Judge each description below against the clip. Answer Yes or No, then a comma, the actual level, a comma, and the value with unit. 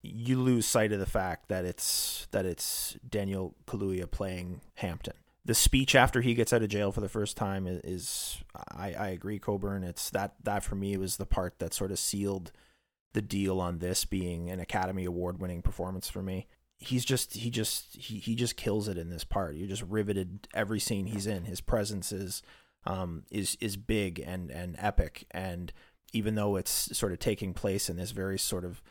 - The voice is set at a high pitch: No, low, 100 Hz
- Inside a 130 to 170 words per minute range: No, average, 195 wpm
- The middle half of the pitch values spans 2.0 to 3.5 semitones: Yes, average, 2.7 semitones